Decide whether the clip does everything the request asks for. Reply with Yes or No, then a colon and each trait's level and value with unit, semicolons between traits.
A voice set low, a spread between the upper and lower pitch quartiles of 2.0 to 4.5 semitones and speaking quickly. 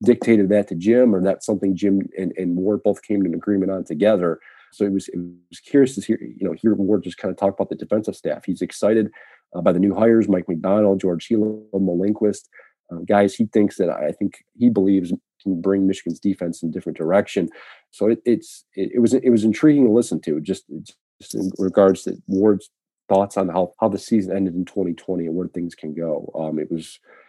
Yes: low, 100 Hz; average, 2.8 semitones; fast, 225 wpm